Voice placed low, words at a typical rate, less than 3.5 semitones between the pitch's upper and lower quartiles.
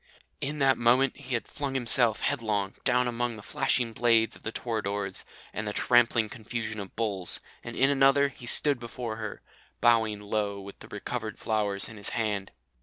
Yes: low, 115 Hz; average, 180 wpm; average, 2.9 semitones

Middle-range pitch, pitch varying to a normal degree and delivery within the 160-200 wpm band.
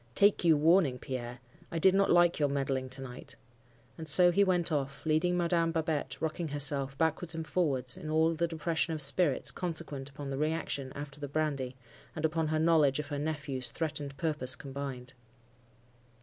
Yes: medium, 150 Hz; average, 3.1 semitones; average, 180 wpm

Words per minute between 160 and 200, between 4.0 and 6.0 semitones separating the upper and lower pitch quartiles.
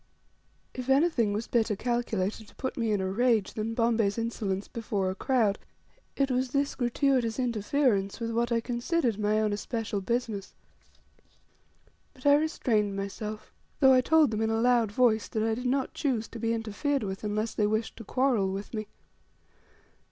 No: average, 175 wpm; average, 3.1 semitones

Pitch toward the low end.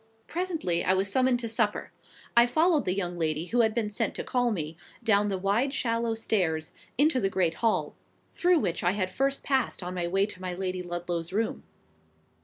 No: high, 205 Hz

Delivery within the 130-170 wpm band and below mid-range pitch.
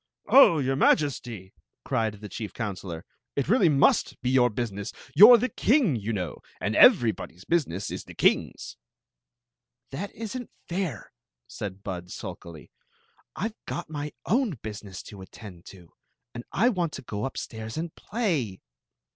Yes: average, 160 wpm; low, 120 Hz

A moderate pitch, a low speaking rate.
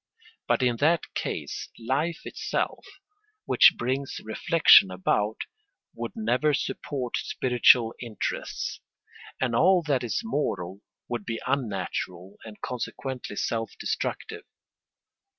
No: low, 125 Hz; slow, 105 wpm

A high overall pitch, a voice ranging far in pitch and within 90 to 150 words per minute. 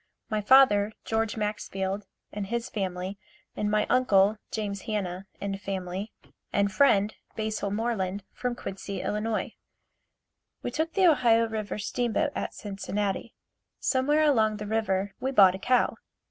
No: high, 210 Hz; average, 2.8 semitones; average, 140 wpm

